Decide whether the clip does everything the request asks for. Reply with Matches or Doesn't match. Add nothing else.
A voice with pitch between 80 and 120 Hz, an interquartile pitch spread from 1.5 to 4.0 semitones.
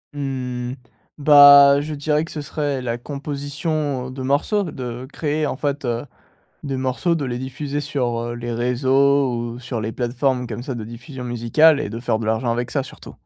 Doesn't match